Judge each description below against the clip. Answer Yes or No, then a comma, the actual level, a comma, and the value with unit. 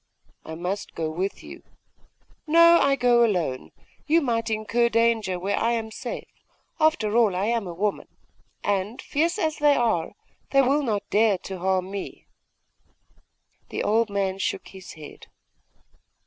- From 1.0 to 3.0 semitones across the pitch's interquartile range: No, average, 4.2 semitones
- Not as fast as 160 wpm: Yes, average, 150 wpm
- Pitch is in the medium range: No, high, 220 Hz